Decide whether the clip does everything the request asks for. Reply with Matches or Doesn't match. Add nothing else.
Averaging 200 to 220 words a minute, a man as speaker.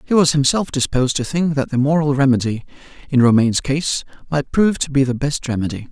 Matches